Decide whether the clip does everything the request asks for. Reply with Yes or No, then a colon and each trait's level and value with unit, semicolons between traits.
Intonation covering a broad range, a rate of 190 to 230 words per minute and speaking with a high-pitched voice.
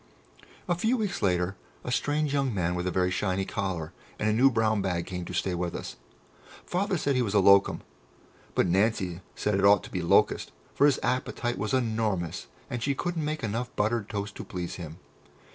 No: wide, 5.7 semitones; average, 200 wpm; low, 105 Hz